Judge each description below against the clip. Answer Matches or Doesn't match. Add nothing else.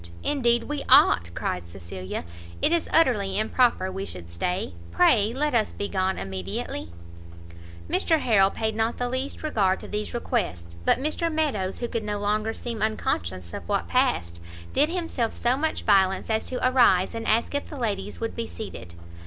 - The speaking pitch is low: Doesn't match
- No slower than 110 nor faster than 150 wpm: Doesn't match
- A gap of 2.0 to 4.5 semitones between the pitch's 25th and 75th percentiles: Doesn't match